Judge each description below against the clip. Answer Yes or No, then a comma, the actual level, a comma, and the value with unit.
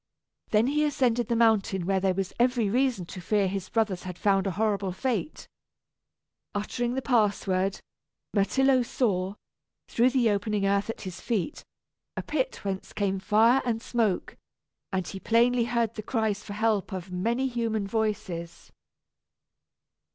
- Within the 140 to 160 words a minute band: Yes, average, 150 wpm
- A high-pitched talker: Yes, high, 215 Hz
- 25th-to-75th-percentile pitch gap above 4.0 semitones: No, average, 3.5 semitones